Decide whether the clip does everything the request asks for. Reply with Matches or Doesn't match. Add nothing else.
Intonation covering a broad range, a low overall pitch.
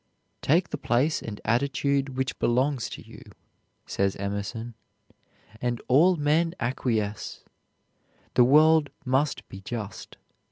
Doesn't match